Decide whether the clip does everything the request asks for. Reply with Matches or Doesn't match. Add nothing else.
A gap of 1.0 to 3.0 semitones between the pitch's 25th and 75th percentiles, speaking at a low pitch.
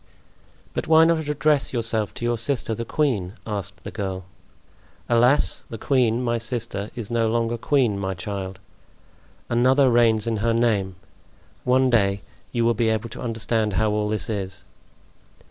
Matches